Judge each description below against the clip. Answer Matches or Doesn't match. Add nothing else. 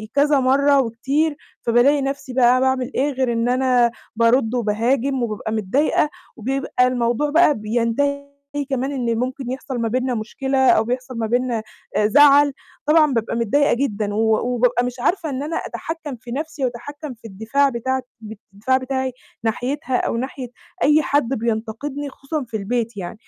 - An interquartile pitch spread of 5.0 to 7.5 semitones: Doesn't match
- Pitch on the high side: Matches